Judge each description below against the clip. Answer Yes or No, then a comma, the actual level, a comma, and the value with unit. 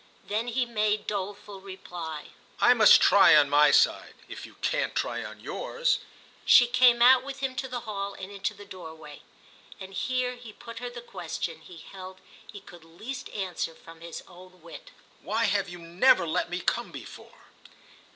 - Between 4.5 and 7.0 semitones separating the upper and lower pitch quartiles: Yes, wide, 5.6 semitones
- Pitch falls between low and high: No, high, 200 Hz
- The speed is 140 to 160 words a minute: No, average, 175 wpm